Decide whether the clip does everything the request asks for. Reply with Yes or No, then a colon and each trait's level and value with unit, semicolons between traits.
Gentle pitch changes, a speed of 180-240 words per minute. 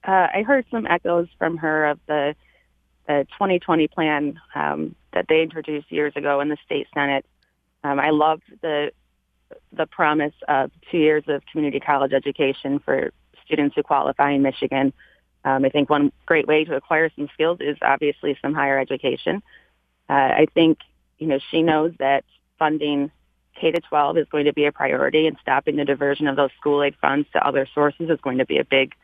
Yes: narrow, 2.1 semitones; average, 190 wpm